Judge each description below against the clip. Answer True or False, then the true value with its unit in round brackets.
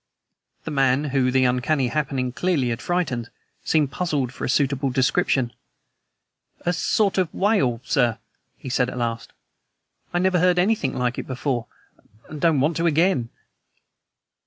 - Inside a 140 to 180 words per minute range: True (150 wpm)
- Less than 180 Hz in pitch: True (135 Hz)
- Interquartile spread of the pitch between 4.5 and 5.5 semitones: True (5.0 semitones)